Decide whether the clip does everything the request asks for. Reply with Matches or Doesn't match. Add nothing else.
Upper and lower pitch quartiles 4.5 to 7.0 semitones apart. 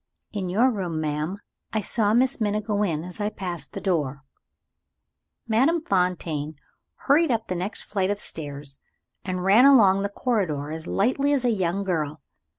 Matches